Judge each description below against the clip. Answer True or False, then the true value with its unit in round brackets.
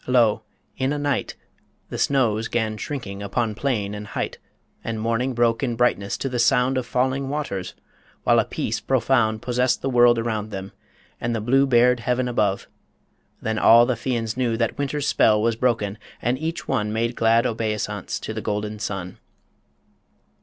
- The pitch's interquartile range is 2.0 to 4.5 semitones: True (2.9 semitones)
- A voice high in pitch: False (115 Hz)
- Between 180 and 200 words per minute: False (170 wpm)